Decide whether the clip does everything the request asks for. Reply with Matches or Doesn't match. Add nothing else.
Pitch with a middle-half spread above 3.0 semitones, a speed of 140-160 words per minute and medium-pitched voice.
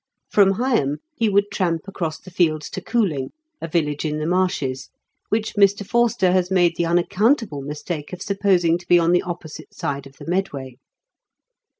Doesn't match